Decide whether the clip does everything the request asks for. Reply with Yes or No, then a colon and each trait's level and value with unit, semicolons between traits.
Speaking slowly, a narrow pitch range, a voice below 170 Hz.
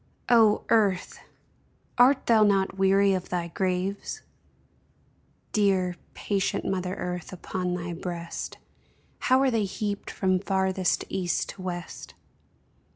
No: slow, 115 wpm; narrow, 2.0 semitones; high, 190 Hz